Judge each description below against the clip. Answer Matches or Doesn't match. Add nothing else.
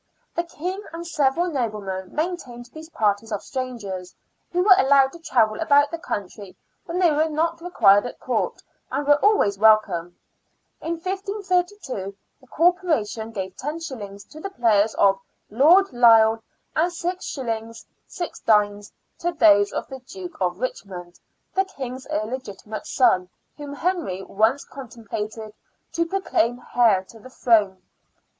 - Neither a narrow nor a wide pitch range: Doesn't match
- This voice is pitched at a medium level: Doesn't match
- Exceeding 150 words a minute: Doesn't match